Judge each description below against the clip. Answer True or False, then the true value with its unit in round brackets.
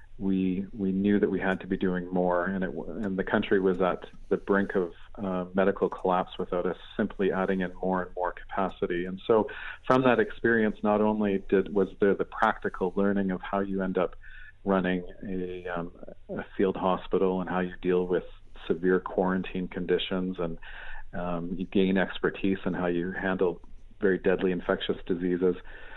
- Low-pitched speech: True (95 Hz)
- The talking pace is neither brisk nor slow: True (180 wpm)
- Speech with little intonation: True (1.2 semitones)